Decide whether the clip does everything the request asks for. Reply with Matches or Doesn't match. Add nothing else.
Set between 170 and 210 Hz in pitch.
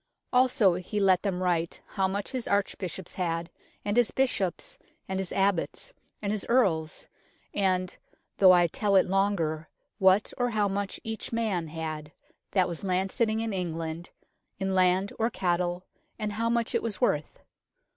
Matches